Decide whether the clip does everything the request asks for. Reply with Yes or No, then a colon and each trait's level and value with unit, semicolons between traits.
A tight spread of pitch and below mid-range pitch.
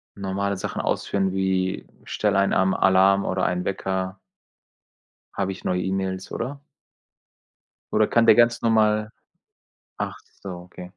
Yes: narrow, 2.0 semitones; very low, 95 Hz